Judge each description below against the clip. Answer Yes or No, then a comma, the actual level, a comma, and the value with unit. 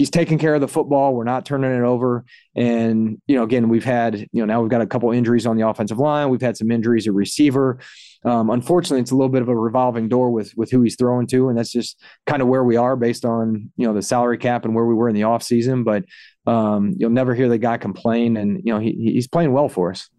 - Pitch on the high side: No, low, 120 Hz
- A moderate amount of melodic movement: No, narrow, 2.0 semitones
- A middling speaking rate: No, fast, 270 wpm